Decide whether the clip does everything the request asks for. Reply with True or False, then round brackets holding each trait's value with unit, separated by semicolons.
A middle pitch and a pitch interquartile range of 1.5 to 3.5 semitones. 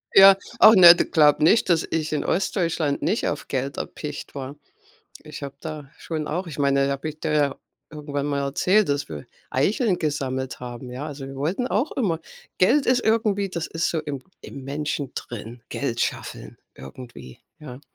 False (150 Hz; 4.0 semitones)